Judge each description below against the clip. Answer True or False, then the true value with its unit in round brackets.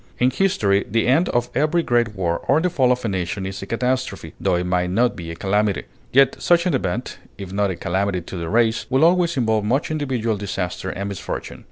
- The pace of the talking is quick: True (220 wpm)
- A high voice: False (110 Hz)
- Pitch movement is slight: False (5.4 semitones)